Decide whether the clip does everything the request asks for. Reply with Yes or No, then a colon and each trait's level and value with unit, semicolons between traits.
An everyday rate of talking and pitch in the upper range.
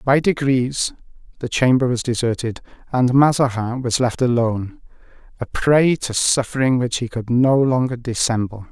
No: average, 145 wpm; low, 125 Hz